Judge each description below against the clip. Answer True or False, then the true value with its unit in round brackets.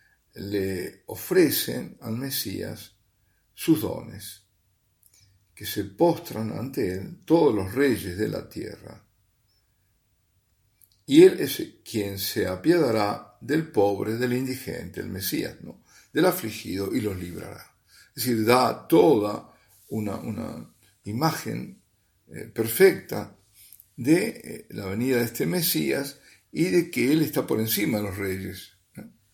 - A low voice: True (105 Hz)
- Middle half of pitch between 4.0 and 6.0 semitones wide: True (4.6 semitones)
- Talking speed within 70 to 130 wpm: True (125 wpm)